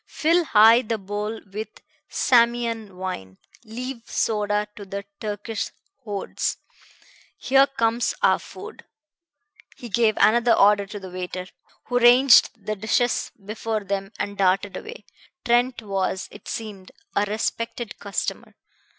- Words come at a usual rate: No, slow, 125 wpm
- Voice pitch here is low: No, high, 215 Hz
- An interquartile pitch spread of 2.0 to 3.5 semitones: Yes, average, 2.9 semitones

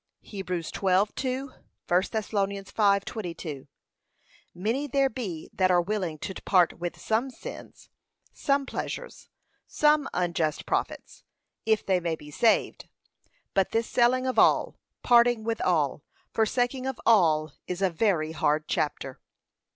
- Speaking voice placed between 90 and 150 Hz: No, high, 200 Hz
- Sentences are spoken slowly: Yes, slow, 130 wpm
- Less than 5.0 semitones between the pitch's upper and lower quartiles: No, wide, 5.5 semitones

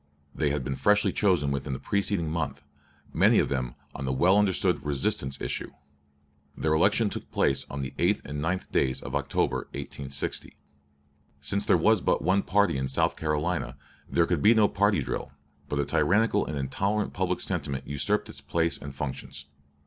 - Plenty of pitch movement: Yes, wide, 6.2 semitones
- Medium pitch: No, very low, 75 Hz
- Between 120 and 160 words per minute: No, average, 175 wpm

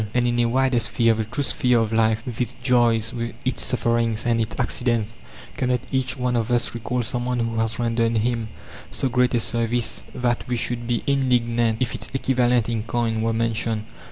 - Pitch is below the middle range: Yes, low, 120 Hz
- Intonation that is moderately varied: No, narrow, 1.4 semitones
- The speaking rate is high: No, average, 190 wpm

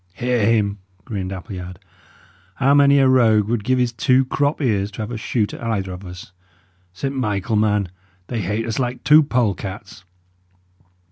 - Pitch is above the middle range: No, low, 110 Hz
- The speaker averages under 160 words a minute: No, average, 165 wpm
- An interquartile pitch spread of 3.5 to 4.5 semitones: Yes, average, 4.0 semitones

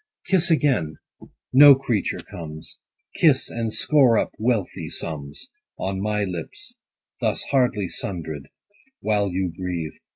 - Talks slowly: Yes, slow, 120 wpm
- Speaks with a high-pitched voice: No, low, 100 Hz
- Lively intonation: Yes, wide, 7.2 semitones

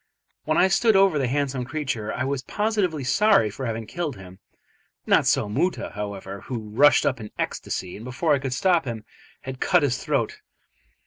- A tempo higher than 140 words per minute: Yes, average, 185 wpm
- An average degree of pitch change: No, wide, 6.8 semitones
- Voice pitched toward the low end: Yes, low, 130 Hz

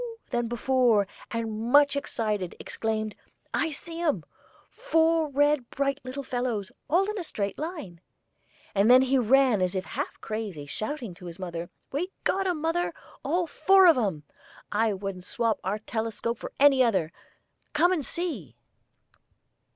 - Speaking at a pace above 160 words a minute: No, average, 150 wpm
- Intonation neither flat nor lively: No, wide, 6.4 semitones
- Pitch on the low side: No, high, 245 Hz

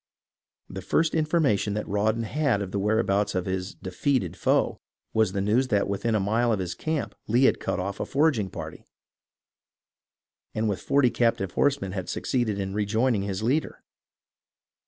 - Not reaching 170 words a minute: No, average, 175 wpm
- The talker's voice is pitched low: Yes, low, 105 Hz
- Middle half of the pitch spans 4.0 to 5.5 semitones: Yes, average, 4.4 semitones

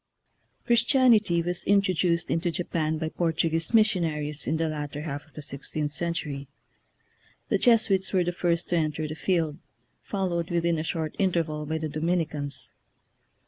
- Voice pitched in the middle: Yes, medium, 165 Hz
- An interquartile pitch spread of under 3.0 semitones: Yes, narrow, 2.6 semitones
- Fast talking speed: No, average, 155 wpm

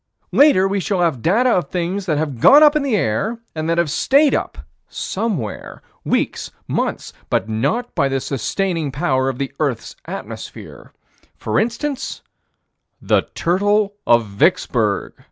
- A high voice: No, medium, 175 Hz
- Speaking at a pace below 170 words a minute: Yes, average, 150 wpm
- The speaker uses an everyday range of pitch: No, wide, 8.0 semitones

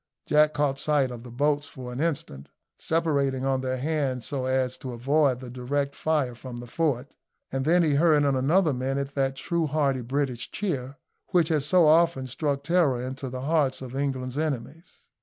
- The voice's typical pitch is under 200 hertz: Yes, medium, 140 Hz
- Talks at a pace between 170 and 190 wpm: Yes, average, 185 wpm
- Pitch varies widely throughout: No, average, 2.9 semitones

